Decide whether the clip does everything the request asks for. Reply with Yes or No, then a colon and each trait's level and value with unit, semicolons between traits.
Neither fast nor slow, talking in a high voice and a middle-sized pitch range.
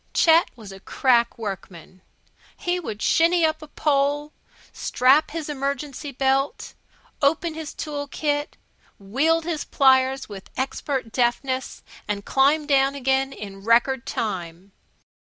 No: slow, 125 wpm; very high, 270 Hz; average, 4.2 semitones